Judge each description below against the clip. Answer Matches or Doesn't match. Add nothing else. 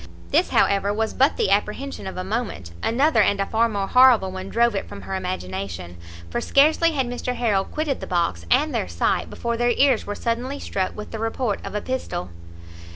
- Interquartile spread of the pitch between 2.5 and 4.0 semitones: Doesn't match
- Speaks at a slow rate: Doesn't match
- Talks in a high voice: Matches